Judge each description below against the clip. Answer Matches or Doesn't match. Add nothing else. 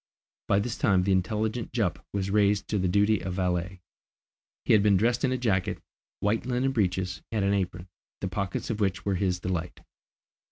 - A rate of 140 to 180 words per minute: Doesn't match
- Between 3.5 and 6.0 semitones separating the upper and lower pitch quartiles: Doesn't match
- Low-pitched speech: Matches